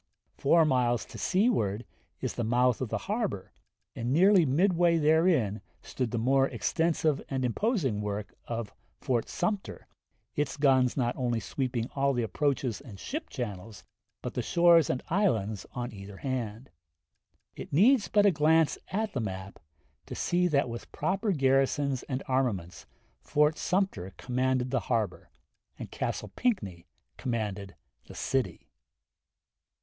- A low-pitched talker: Yes, low, 130 Hz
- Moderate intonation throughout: No, wide, 6.2 semitones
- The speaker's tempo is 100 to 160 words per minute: Yes, average, 140 wpm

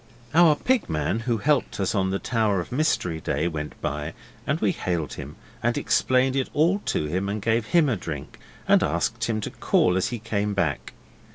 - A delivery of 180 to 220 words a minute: Yes, average, 200 wpm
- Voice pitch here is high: No, low, 105 Hz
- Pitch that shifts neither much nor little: No, wide, 6.5 semitones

